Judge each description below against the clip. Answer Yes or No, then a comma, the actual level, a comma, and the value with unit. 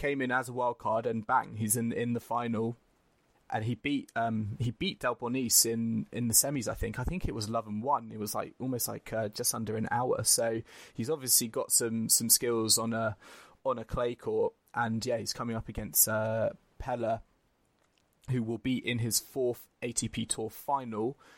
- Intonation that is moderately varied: No, narrow, 1.6 semitones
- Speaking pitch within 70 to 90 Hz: No, low, 115 Hz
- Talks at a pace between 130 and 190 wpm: No, average, 200 wpm